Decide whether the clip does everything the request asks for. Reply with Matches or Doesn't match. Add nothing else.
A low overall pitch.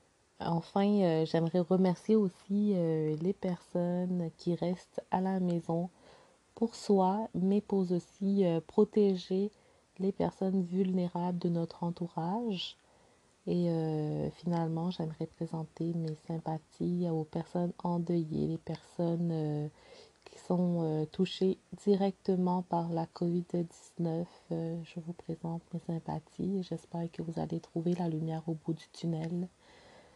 Doesn't match